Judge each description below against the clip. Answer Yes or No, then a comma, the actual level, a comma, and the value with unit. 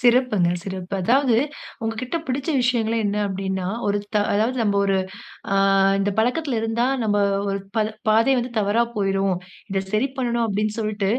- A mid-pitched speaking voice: No, high, 215 Hz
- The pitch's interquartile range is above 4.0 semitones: No, average, 3.4 semitones